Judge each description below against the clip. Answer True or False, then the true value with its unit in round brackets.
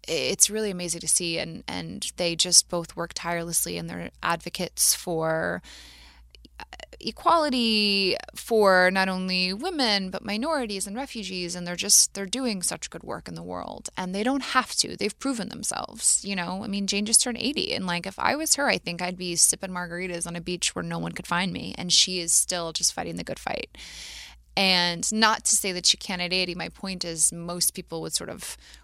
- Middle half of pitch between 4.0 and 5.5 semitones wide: False (3.4 semitones)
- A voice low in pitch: False (185 Hz)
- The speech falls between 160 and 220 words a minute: True (205 wpm)